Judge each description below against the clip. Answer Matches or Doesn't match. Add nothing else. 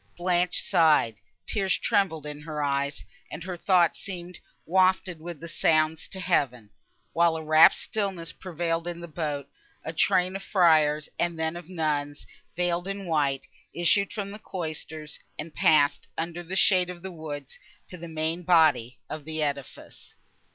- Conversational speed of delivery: Matches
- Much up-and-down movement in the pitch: Doesn't match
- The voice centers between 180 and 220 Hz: Doesn't match